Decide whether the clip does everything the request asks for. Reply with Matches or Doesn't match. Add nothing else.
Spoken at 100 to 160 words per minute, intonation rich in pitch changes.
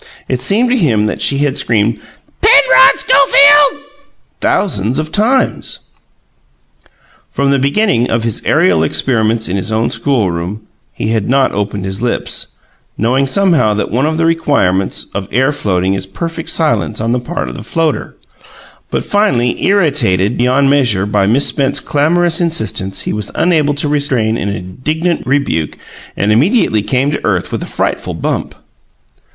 Matches